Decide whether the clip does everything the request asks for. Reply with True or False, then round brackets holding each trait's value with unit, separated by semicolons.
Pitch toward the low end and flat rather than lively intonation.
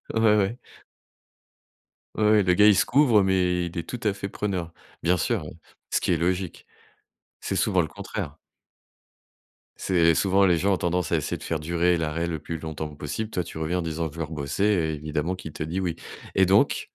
False (90 Hz; 3.1 semitones)